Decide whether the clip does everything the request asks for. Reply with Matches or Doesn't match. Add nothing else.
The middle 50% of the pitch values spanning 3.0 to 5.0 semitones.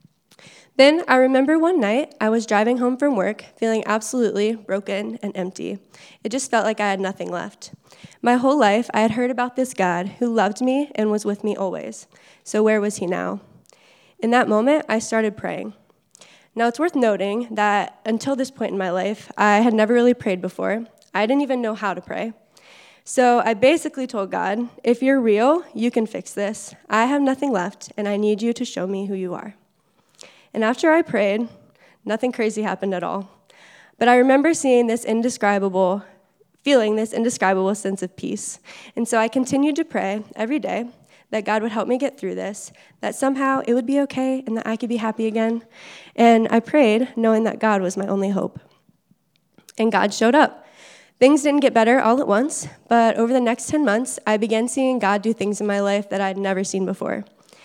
Matches